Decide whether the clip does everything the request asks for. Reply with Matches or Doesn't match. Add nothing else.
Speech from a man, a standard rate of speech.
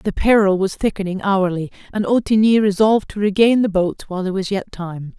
Doesn't match